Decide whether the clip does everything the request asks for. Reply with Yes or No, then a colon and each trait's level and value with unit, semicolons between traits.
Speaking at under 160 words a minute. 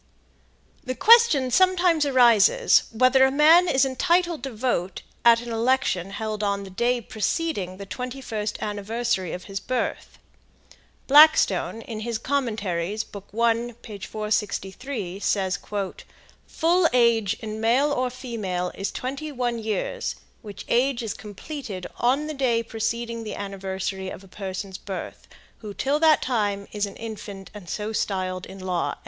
Yes: average, 145 wpm